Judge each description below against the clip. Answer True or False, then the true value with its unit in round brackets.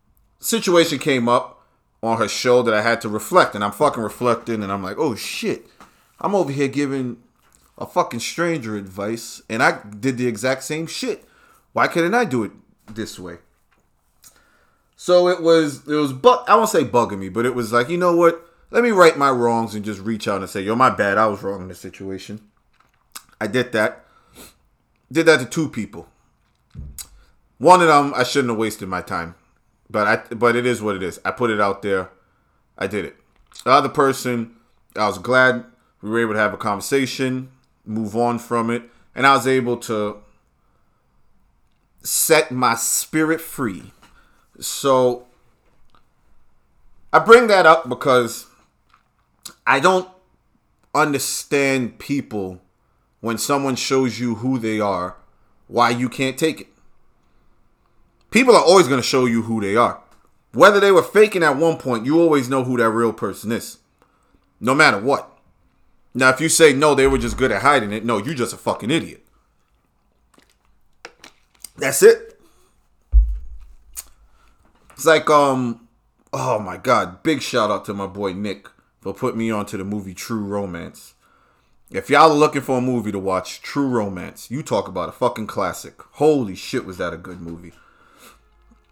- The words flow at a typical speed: True (170 wpm)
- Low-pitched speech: True (120 Hz)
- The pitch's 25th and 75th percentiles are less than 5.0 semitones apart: False (5.3 semitones)